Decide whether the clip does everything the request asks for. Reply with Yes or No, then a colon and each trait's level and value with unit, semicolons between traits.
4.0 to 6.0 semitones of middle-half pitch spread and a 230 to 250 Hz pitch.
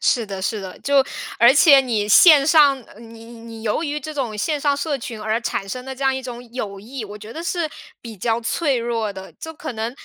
Yes: average, 4.3 semitones; high, 240 Hz